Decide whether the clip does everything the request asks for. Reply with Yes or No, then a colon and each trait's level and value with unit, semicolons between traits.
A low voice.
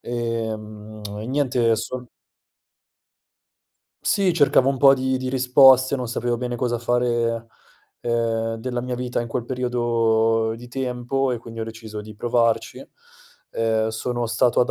Yes: low, 120 Hz